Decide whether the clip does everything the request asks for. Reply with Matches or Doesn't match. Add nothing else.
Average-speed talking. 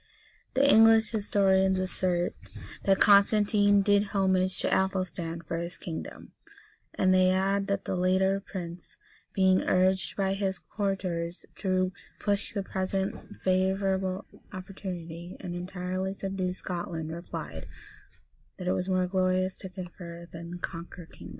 Doesn't match